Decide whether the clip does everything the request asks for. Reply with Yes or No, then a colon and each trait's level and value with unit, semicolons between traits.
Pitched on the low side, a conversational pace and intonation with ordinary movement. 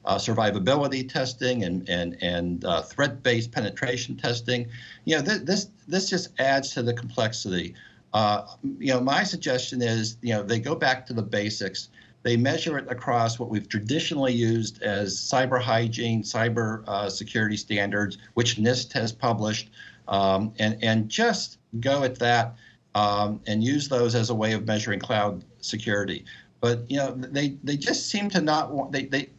Yes: low, 120 Hz; average, 170 wpm; average, 4.0 semitones